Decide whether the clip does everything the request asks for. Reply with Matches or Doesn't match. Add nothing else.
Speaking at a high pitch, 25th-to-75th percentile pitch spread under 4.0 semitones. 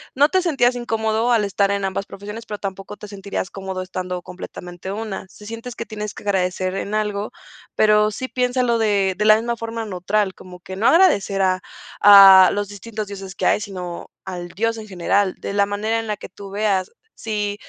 Matches